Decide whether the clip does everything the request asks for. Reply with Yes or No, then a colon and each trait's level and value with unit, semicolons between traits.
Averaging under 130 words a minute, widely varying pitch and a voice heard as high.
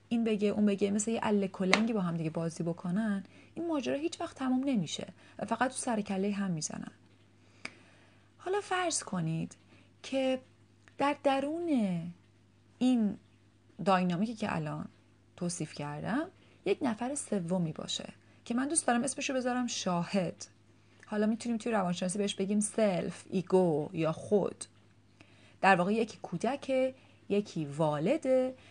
No: average, 135 wpm; wide, 6.8 semitones; high, 205 Hz